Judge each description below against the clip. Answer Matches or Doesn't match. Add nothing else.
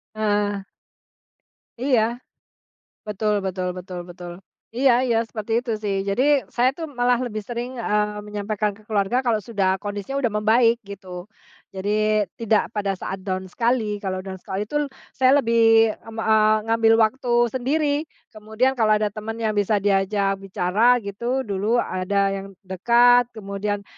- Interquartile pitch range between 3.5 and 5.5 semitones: Doesn't match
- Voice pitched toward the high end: Matches